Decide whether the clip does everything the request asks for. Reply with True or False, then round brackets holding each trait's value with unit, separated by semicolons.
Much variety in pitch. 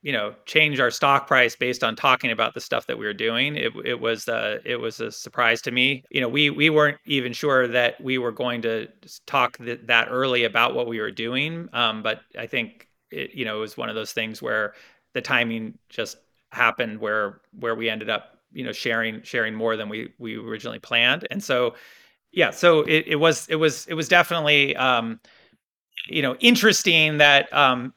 False (4.2 semitones)